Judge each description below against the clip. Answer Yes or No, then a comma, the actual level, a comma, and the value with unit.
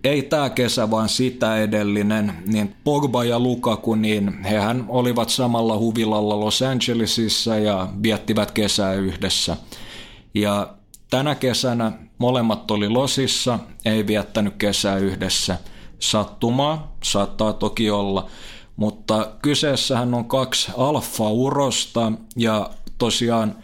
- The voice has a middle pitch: No, low, 110 Hz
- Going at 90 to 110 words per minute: Yes, average, 105 wpm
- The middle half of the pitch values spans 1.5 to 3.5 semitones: Yes, average, 2.8 semitones